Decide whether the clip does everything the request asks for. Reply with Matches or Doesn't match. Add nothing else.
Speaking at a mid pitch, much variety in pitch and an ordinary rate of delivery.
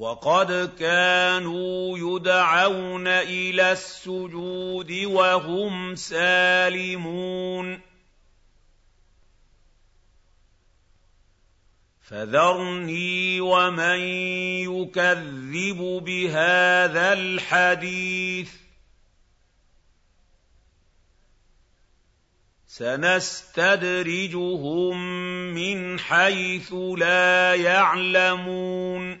Doesn't match